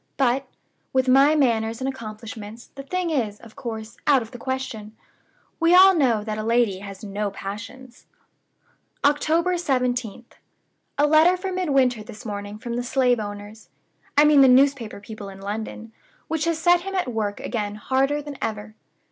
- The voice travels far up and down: No, average, 4.9 semitones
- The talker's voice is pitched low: No, high, 245 Hz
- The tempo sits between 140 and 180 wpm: Yes, average, 165 wpm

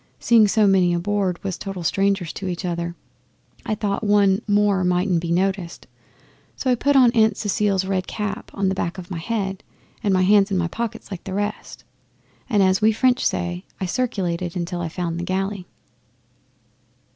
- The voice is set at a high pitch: Yes, high, 195 Hz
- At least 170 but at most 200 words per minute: Yes, average, 180 wpm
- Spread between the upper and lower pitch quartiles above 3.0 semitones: No, narrow, 2.6 semitones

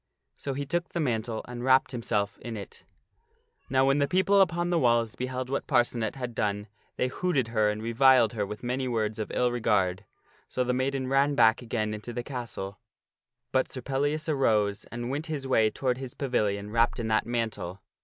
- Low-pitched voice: Yes, low, 120 Hz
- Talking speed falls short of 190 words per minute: No, average, 195 wpm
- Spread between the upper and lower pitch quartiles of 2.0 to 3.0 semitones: No, average, 3.5 semitones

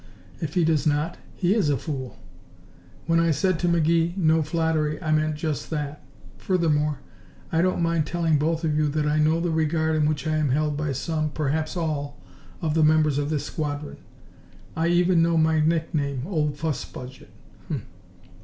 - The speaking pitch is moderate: Yes, medium, 155 Hz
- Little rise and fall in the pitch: Yes, narrow, 1.7 semitones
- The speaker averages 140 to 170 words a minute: No, average, 180 wpm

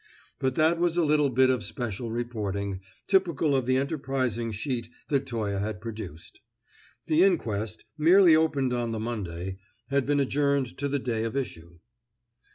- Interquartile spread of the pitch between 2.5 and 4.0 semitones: No, average, 4.6 semitones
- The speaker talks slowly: No, average, 160 wpm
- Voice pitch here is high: No, low, 125 Hz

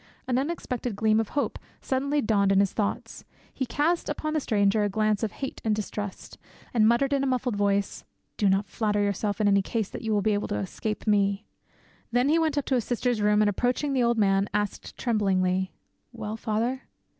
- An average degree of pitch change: Yes, average, 3.7 semitones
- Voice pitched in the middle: No, high, 215 Hz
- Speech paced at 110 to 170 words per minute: No, fast, 205 wpm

